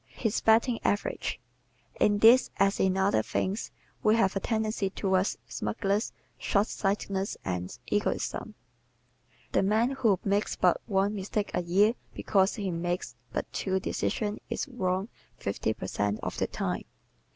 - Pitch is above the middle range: Yes, high, 195 Hz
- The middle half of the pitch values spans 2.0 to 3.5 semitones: Yes, narrow, 2.5 semitones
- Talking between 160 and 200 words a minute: No, average, 145 wpm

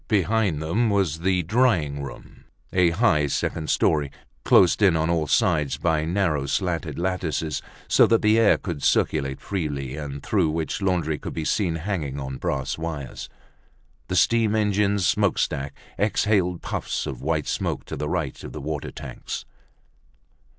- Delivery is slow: No, average, 155 wpm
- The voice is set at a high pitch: No, very low, 80 Hz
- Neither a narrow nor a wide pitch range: Yes, average, 4.8 semitones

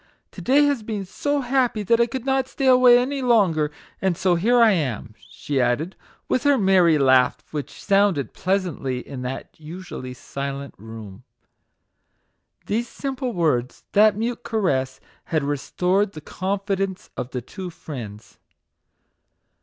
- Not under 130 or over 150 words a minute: Yes, average, 145 wpm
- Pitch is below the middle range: No, medium, 185 Hz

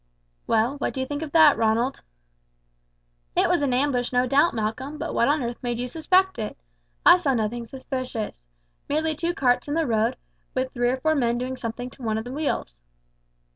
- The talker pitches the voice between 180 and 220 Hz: No, very high, 255 Hz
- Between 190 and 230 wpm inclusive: Yes, average, 200 wpm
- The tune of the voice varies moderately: Yes, average, 3.6 semitones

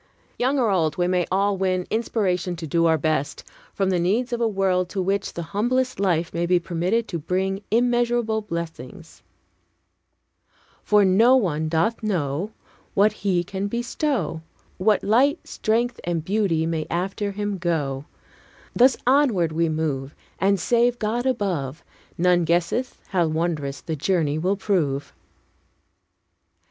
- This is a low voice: No, medium, 185 Hz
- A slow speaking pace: No, average, 145 wpm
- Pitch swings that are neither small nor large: Yes, average, 4.7 semitones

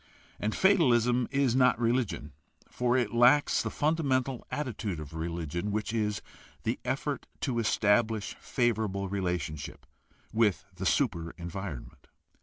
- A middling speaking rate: No, slow, 120 wpm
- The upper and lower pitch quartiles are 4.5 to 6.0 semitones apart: Yes, wide, 5.5 semitones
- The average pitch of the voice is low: Yes, low, 110 Hz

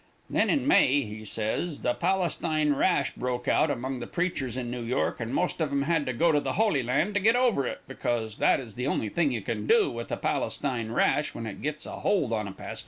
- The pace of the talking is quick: Yes, fast, 240 wpm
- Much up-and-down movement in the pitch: Yes, wide, 5.7 semitones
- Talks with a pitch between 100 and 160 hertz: Yes, low, 135 Hz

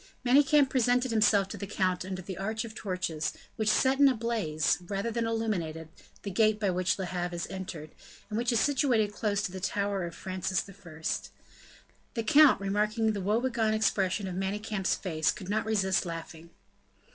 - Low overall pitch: No, high, 205 Hz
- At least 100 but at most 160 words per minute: No, average, 180 wpm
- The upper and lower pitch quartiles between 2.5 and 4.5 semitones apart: Yes, average, 3.4 semitones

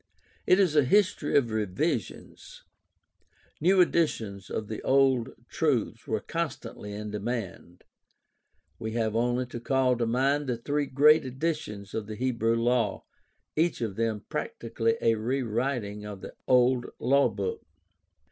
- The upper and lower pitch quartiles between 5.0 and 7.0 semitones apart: No, average, 4.1 semitones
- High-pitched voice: No, low, 120 Hz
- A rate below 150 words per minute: Yes, average, 140 wpm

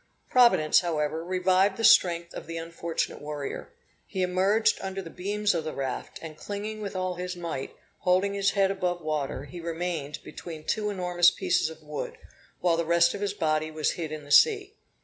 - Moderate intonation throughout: Yes, average, 3.5 semitones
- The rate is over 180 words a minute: Yes, average, 190 wpm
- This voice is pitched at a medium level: Yes, medium, 175 Hz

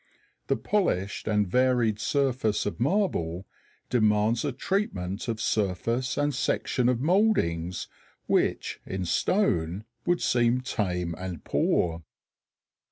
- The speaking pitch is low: Yes, low, 110 Hz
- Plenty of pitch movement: Yes, wide, 5.9 semitones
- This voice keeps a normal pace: No, slow, 110 wpm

